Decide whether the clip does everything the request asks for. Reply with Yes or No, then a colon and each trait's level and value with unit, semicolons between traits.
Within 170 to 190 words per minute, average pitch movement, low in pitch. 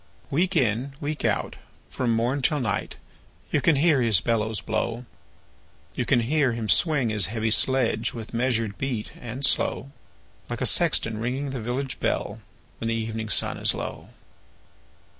No: average, 160 wpm; average, 3.4 semitones; low, 120 Hz